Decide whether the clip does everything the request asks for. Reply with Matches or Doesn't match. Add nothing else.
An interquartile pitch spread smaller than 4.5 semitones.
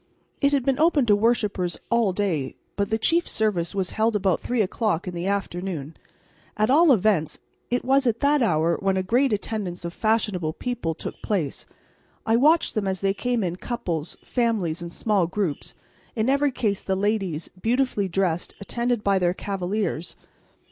Doesn't match